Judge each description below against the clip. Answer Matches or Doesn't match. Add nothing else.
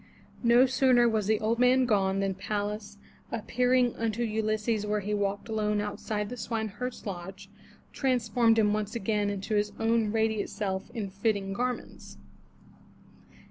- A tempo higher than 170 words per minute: Doesn't match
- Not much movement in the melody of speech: Matches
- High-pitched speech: Matches